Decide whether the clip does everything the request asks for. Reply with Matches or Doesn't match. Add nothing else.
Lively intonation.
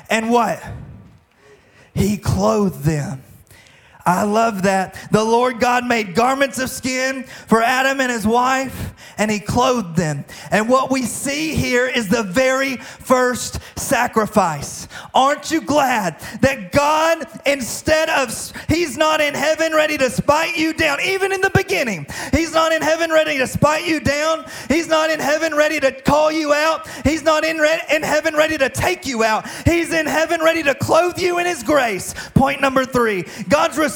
Matches